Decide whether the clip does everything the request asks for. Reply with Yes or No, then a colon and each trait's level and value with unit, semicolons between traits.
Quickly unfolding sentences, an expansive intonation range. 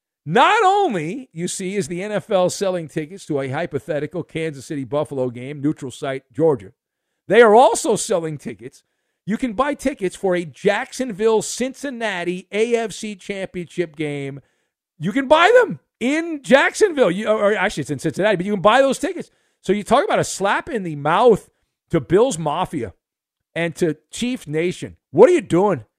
No: average, 170 wpm; wide, 7.0 semitones